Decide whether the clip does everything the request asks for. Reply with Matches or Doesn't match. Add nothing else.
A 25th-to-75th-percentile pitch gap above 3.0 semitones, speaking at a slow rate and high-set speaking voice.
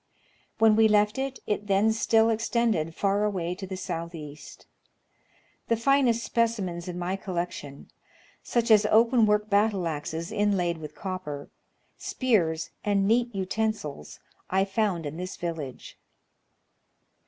Matches